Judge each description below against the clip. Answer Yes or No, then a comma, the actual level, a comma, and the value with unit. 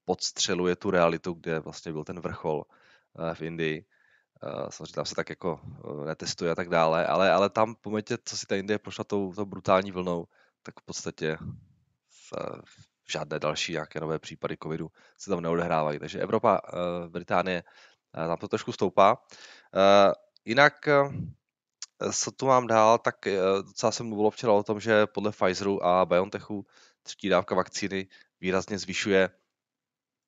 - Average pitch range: Yes, average, 4.2 semitones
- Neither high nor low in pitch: No, very low, 95 Hz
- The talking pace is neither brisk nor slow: Yes, average, 150 wpm